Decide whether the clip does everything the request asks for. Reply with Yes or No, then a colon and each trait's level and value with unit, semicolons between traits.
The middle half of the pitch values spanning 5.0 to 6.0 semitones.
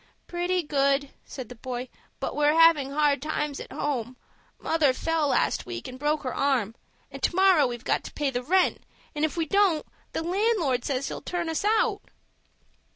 No: average, 4.1 semitones